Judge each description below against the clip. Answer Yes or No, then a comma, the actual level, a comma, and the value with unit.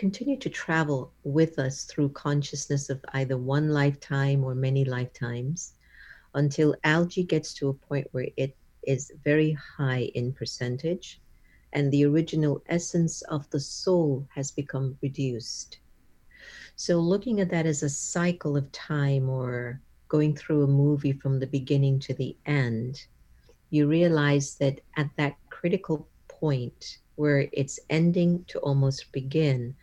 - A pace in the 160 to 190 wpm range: No, average, 140 wpm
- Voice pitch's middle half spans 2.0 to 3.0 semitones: Yes, narrow, 2.5 semitones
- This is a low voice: No, medium, 145 Hz